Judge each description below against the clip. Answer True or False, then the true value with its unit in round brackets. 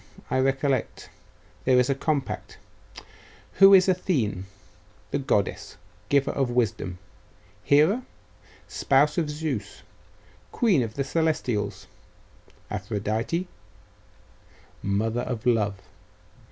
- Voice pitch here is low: True (130 Hz)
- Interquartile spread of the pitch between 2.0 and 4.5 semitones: False (5.6 semitones)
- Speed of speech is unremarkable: False (95 wpm)